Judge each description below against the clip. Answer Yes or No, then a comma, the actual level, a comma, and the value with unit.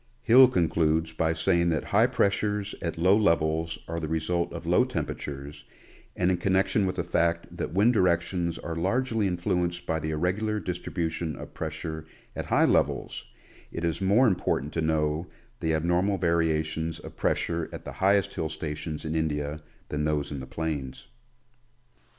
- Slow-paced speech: No, average, 160 wpm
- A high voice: No, very low, 85 Hz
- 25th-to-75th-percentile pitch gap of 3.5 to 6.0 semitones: No, average, 2.7 semitones